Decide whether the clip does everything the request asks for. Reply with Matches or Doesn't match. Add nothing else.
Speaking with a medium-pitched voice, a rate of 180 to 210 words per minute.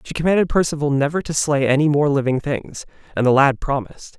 Matches